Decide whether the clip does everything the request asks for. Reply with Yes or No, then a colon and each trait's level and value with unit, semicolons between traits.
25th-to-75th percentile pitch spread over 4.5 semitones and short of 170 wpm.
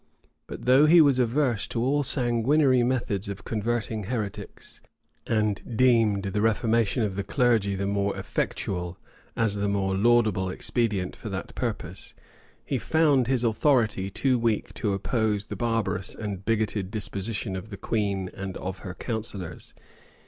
No: average, 3.4 semitones; average, 150 wpm